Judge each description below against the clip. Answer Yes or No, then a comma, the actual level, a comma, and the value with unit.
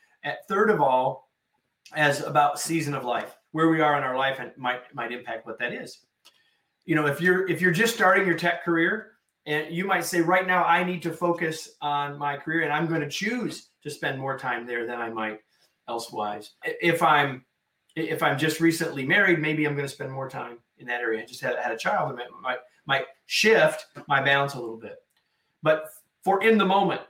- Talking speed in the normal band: No, fast, 215 wpm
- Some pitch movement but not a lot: Yes, average, 4.1 semitones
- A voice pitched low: No, medium, 150 Hz